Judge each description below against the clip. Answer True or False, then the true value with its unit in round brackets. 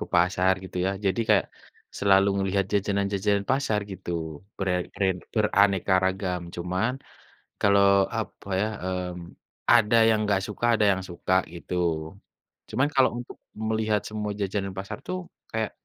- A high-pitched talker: False (100 Hz)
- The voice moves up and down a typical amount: False (2.3 semitones)